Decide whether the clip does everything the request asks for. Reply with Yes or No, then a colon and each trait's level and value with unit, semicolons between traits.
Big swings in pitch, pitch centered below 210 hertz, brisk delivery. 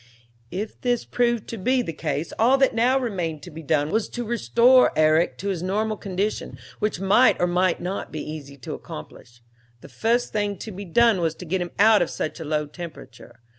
Yes: wide, 5.9 semitones; high, 190 Hz; fast, 210 wpm